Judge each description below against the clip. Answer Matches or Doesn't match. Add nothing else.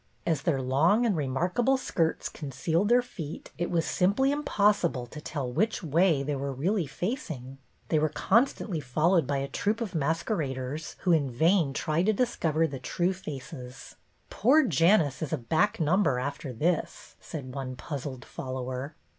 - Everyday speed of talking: Matches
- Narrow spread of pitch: Doesn't match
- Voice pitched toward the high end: Doesn't match